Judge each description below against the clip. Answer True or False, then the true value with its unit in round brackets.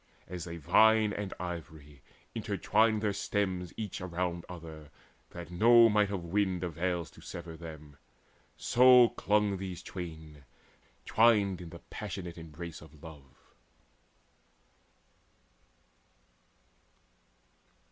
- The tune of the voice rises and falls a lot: False (3.7 semitones)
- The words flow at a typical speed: False (105 wpm)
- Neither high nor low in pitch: False (90 Hz)